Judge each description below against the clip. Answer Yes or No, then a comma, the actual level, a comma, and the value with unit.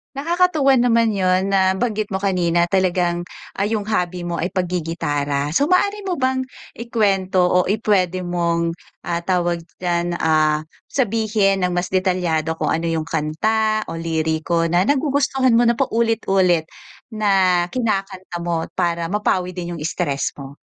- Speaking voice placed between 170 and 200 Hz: Yes, medium, 185 Hz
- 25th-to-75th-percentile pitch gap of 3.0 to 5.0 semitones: Yes, average, 4.2 semitones